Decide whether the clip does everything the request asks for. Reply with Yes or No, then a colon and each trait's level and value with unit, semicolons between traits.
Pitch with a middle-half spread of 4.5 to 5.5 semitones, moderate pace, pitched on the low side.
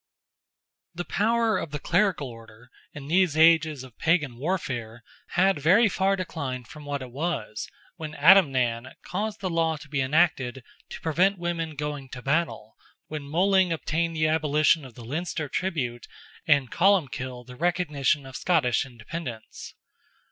No: average, 4.9 semitones; average, 150 wpm; medium, 155 Hz